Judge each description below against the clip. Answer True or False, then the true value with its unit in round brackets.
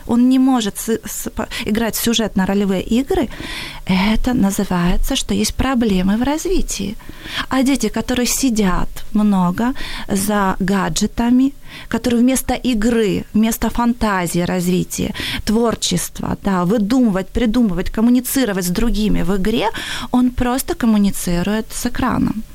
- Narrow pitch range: False (3.8 semitones)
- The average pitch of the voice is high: True (225 Hz)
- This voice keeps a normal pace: True (115 wpm)